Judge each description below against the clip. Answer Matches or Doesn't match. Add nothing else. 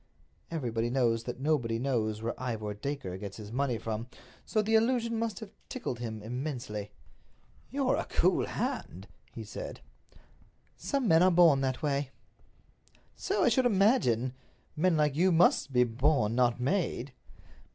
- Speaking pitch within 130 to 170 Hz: Matches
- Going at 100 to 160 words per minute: Matches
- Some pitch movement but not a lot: Doesn't match